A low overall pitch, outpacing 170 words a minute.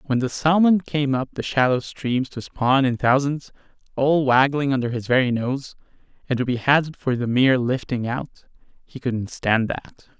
Yes: low, 130 Hz; average, 180 wpm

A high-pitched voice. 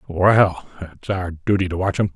No: very low, 95 Hz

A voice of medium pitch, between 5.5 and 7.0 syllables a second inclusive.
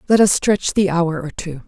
No: medium, 180 Hz; 4.7 syllables/s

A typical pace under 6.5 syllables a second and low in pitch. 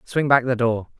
Yes: 4.8 syllables/s; low, 125 Hz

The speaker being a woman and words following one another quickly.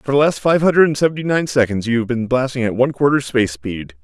No: male; fast, 270 wpm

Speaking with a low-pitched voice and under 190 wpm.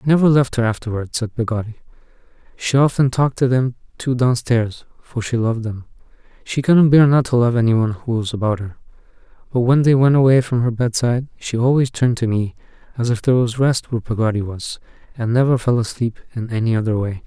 No: low, 120 Hz; average, 200 wpm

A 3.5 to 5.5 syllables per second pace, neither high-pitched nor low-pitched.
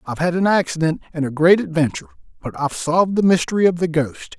No: 6.8 syllables/s; medium, 160 Hz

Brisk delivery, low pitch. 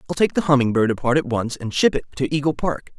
Yes: fast, 280 wpm; low, 130 Hz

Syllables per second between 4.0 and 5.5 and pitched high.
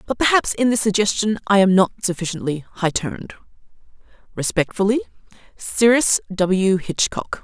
Yes: 5.0 syllables/s; high, 200 Hz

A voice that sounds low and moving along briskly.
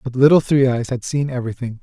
Yes: low, 130 Hz; fast, 230 wpm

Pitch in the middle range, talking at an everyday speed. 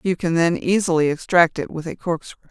No: medium, 165 Hz; fast, 215 wpm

